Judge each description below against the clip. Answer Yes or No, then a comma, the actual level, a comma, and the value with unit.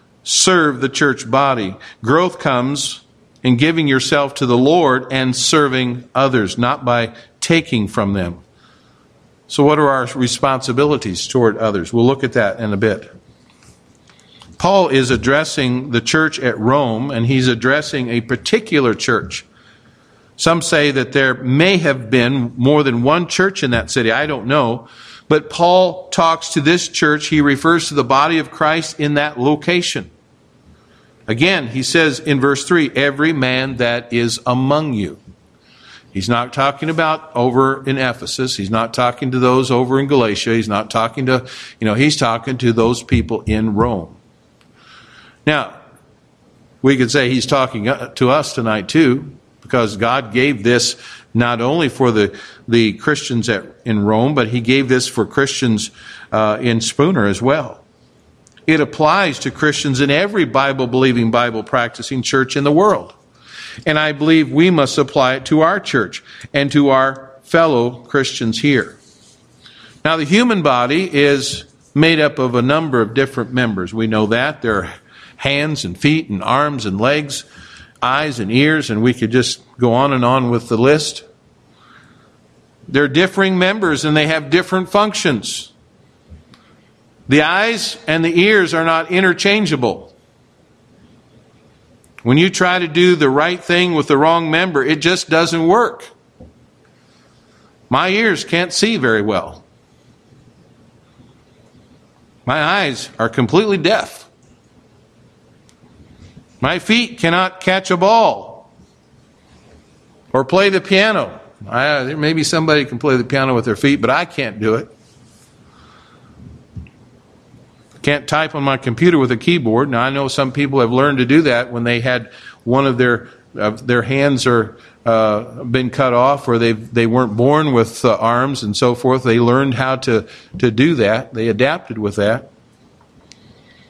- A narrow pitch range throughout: No, average, 4.2 semitones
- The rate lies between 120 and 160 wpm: Yes, average, 155 wpm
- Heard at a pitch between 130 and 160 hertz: Yes, low, 135 Hz